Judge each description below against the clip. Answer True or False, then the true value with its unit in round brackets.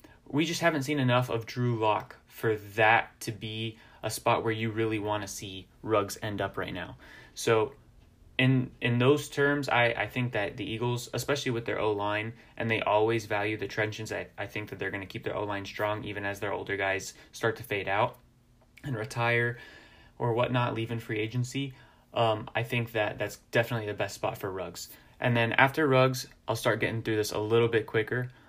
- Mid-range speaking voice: False (115 Hz)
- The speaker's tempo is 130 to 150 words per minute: False (205 wpm)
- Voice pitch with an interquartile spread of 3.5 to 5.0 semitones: False (2.5 semitones)